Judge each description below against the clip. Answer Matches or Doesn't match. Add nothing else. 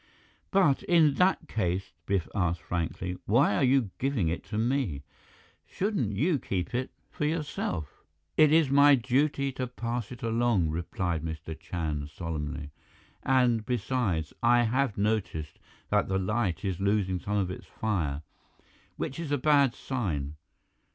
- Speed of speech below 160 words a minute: Matches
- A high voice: Doesn't match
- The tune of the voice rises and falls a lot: Matches